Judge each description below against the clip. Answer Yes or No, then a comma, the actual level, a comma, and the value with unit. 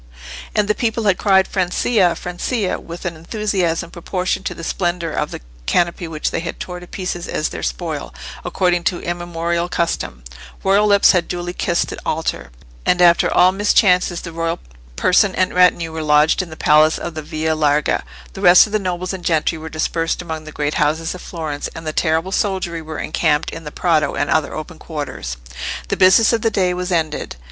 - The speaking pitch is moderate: Yes, medium, 175 Hz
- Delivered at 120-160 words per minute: No, average, 195 wpm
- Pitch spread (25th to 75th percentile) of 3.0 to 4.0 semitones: No, narrow, 2.6 semitones